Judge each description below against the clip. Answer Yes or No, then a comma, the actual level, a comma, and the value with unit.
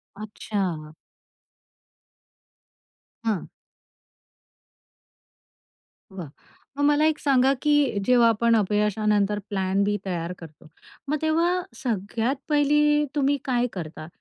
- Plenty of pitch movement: Yes, wide, 6.6 semitones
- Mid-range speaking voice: No, high, 225 Hz